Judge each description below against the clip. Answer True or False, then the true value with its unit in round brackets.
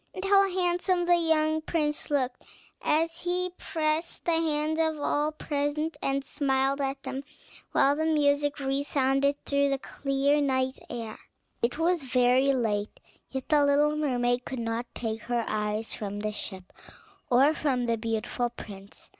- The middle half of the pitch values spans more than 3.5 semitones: True (4.0 semitones)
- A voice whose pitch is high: True (280 Hz)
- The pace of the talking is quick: False (155 wpm)